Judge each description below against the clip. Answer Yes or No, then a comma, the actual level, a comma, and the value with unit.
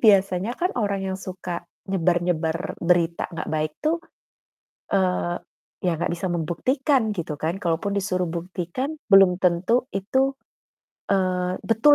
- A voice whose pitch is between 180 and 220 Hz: Yes, medium, 185 Hz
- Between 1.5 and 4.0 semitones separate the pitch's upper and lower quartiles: Yes, average, 2.9 semitones